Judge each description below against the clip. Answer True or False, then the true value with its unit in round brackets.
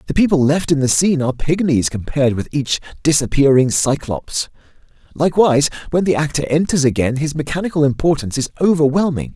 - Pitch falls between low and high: True (145 Hz)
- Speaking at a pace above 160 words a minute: False (155 wpm)